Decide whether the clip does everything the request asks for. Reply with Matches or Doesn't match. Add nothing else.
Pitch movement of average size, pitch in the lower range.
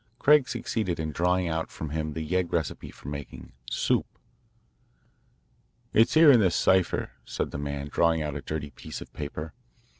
Matches